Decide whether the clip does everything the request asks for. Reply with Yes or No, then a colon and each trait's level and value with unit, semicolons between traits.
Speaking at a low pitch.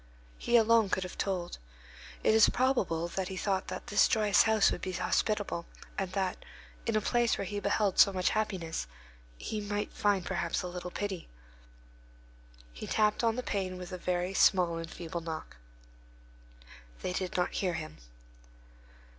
No: high, 190 Hz